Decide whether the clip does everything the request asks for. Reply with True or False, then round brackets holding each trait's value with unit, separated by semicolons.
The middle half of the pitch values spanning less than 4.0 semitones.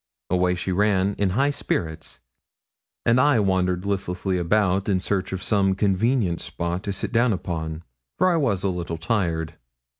True (2.9 semitones)